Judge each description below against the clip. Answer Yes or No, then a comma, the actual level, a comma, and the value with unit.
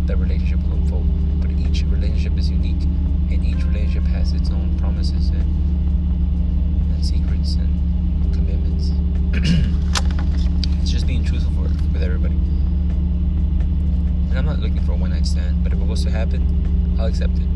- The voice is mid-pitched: No, very low, 80 Hz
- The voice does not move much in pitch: Yes, narrow, 0.8 semitones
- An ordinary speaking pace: Yes, average, 155 wpm